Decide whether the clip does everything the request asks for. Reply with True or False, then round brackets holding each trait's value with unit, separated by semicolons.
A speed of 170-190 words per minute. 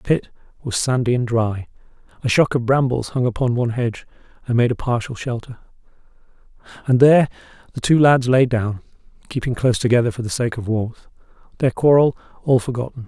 True (175 wpm)